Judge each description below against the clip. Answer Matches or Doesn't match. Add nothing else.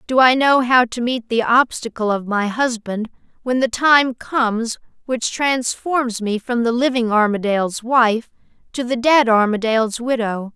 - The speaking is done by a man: Doesn't match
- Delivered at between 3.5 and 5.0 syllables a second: Matches